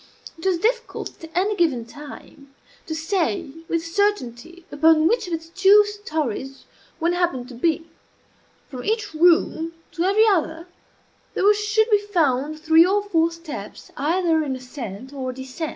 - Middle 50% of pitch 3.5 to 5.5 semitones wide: Yes, average, 5.0 semitones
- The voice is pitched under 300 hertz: No, very high, 330 Hz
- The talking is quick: No, average, 160 wpm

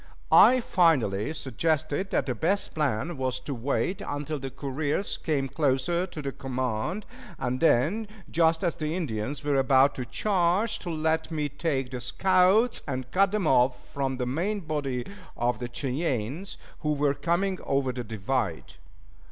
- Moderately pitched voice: Yes, medium, 145 Hz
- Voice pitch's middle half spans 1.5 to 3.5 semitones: No, average, 4.8 semitones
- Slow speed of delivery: No, average, 160 wpm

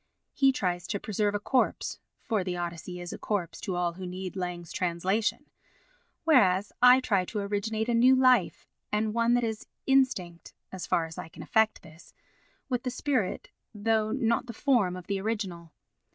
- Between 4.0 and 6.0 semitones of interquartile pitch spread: Yes, average, 4.6 semitones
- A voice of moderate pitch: No, high, 205 Hz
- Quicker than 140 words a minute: Yes, average, 180 wpm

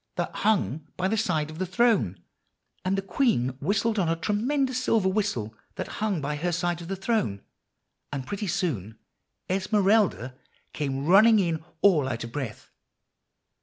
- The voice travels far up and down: Yes, wide, 6.1 semitones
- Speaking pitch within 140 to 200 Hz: Yes, medium, 185 Hz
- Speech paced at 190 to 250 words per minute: No, average, 160 wpm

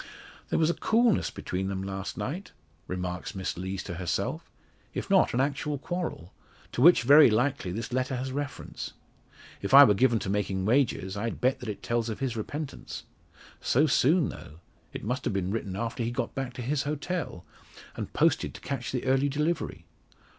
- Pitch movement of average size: No, wide, 6.3 semitones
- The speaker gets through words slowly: No, average, 185 wpm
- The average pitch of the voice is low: Yes, low, 125 Hz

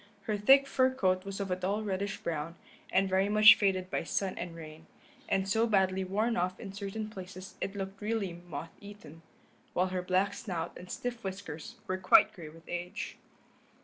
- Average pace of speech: Yes, average, 185 wpm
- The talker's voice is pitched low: No, high, 190 Hz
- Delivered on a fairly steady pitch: Yes, narrow, 2.2 semitones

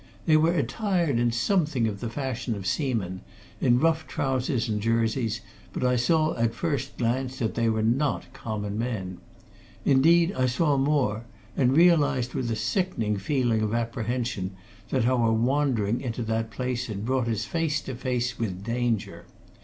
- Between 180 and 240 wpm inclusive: No, average, 160 wpm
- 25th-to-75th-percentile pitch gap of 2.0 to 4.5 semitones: Yes, average, 3.6 semitones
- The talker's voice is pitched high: No, low, 120 Hz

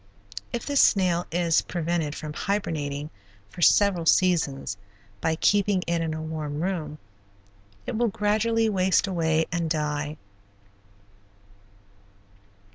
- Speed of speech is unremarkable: No, slow, 115 wpm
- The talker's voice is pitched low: No, medium, 170 Hz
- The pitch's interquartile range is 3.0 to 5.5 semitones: Yes, average, 3.8 semitones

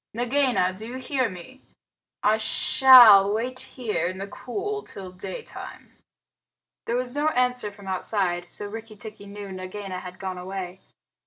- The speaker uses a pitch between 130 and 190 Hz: No, high, 210 Hz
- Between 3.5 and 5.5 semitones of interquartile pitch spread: Yes, average, 4.9 semitones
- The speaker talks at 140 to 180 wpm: Yes, average, 150 wpm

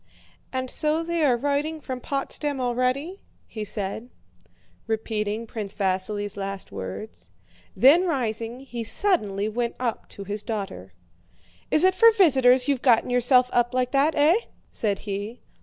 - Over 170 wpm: No, average, 140 wpm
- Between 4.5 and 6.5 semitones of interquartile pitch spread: Yes, average, 5.2 semitones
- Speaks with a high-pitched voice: Yes, high, 245 Hz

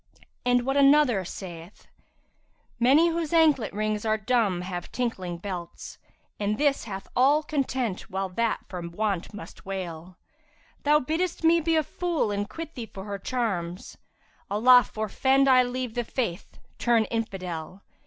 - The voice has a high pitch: Yes, high, 225 Hz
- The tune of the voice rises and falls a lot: Yes, wide, 5.8 semitones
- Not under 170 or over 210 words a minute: No, average, 155 wpm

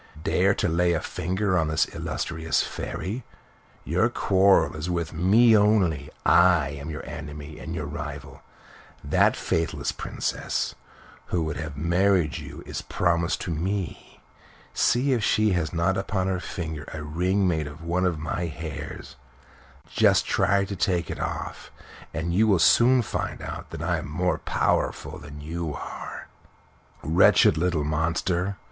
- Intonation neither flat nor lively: Yes, average, 3.3 semitones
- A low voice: Yes, very low, 85 Hz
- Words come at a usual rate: Yes, average, 155 wpm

